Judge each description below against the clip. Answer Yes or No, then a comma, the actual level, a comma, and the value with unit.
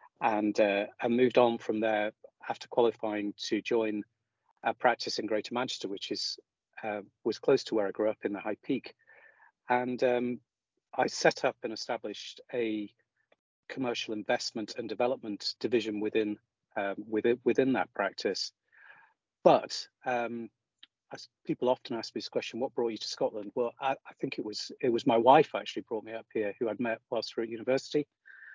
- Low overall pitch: Yes, low, 120 Hz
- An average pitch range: Yes, average, 3.6 semitones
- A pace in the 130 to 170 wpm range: No, average, 180 wpm